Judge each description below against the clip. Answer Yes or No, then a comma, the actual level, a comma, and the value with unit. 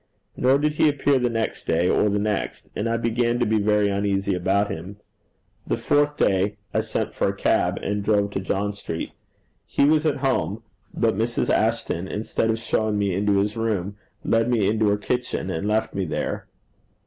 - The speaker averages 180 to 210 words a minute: Yes, average, 195 wpm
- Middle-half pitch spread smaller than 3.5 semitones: Yes, average, 2.7 semitones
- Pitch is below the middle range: Yes, low, 105 Hz